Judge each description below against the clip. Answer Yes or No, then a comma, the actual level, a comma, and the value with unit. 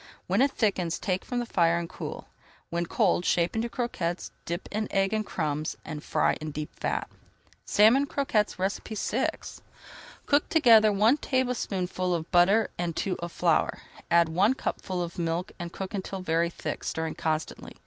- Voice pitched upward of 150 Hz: Yes, medium, 185 Hz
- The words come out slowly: No, average, 165 wpm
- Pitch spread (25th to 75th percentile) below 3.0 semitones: No, average, 4.3 semitones